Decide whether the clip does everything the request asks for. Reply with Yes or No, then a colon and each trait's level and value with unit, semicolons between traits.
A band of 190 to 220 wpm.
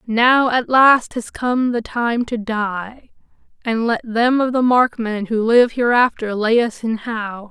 No: average, 175 wpm